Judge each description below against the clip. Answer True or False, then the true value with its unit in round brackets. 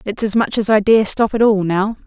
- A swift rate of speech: True (290 wpm)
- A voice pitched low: False (210 Hz)